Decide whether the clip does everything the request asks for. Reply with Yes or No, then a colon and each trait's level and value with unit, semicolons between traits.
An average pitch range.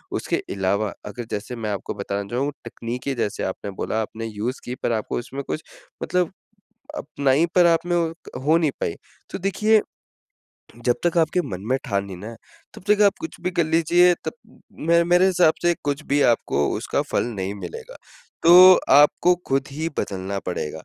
No: wide, 8.4 semitones